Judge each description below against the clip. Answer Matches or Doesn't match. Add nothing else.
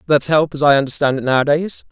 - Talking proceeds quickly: Matches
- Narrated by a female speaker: Doesn't match